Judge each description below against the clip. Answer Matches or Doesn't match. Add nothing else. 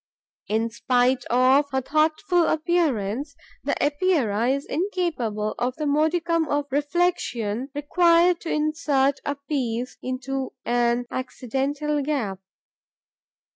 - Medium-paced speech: Doesn't match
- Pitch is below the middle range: Doesn't match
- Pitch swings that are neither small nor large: Matches